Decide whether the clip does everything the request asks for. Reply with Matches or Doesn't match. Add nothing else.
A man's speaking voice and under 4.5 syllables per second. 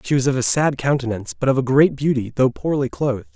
Doesn't match